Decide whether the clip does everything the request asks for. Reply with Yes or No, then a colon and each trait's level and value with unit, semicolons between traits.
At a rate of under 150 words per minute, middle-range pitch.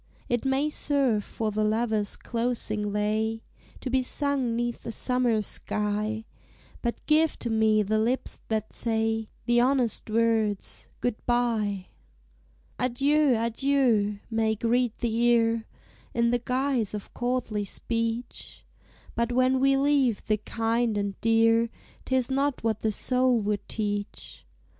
No: slow, 135 wpm; high, 230 Hz